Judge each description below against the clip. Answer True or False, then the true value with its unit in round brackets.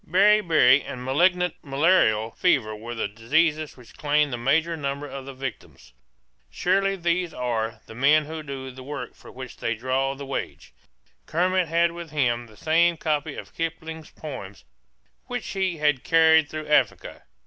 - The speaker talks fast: False (160 wpm)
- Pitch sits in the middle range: True (150 Hz)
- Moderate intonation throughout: True (4.3 semitones)